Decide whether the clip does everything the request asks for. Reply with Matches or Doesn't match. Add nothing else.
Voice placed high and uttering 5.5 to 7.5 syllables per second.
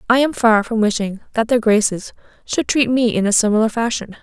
Matches